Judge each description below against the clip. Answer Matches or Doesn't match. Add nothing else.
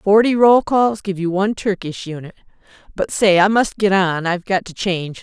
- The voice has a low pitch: Doesn't match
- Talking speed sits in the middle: Matches